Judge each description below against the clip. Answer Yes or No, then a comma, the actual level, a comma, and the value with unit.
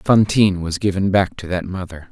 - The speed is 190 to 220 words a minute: Yes, average, 200 wpm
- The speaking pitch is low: Yes, very low, 95 Hz